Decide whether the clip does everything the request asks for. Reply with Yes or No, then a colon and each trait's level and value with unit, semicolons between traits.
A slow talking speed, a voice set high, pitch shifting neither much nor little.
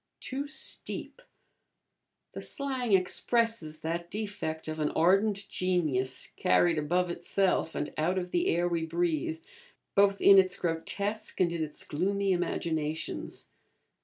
No: slow, 130 wpm; medium, 175 Hz; average, 3.6 semitones